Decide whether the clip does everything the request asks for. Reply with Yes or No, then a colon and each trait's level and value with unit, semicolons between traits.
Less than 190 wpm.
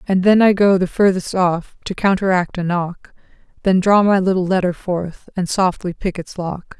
No: average, 195 wpm